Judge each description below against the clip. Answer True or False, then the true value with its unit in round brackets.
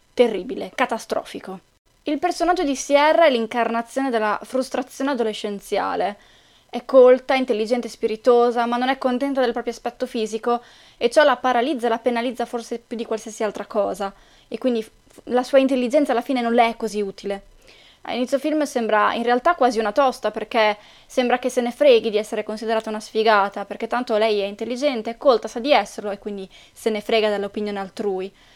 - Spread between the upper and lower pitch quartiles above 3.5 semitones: False (2.8 semitones)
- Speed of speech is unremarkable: False (180 wpm)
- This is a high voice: True (235 Hz)